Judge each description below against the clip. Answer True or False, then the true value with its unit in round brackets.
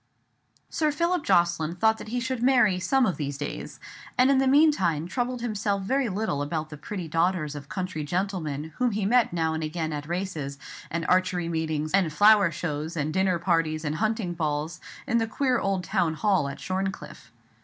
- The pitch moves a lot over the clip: True (5.8 semitones)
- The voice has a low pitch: False (180 Hz)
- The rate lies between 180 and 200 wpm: True (185 wpm)